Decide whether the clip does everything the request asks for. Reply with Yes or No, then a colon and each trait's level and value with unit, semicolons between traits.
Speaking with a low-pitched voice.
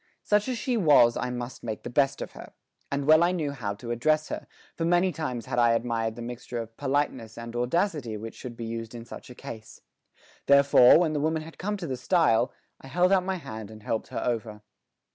Yes: low, 125 Hz